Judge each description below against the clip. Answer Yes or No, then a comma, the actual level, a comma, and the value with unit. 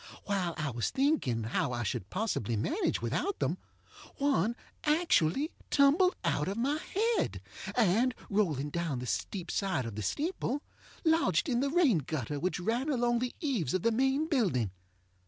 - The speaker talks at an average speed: Yes, average, 160 wpm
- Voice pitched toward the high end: Yes, high, 215 Hz